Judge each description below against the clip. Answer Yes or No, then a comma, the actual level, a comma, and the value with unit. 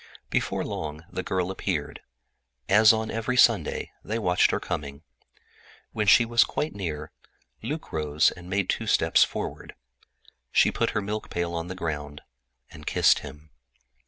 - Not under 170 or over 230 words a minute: No, average, 155 wpm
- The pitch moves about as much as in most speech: No, wide, 5.7 semitones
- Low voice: Yes, very low, 90 Hz